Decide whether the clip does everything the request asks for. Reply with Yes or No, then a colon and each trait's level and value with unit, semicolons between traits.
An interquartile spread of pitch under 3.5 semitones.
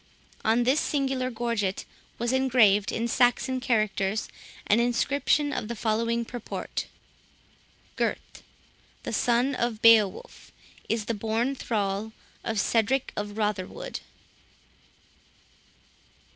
Yes: average, 2.7 semitones